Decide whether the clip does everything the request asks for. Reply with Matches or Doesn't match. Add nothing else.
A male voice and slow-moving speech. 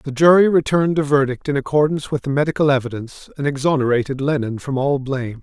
Doesn't match